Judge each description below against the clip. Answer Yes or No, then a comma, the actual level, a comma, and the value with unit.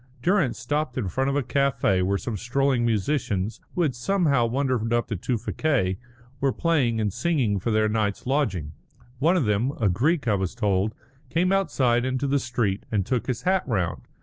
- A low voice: Yes, low, 120 Hz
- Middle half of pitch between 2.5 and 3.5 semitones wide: No, average, 4.8 semitones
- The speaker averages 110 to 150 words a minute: No, average, 185 wpm